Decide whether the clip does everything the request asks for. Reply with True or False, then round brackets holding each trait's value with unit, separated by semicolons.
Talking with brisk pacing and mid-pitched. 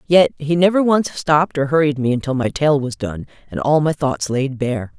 True (230 wpm; 145 Hz)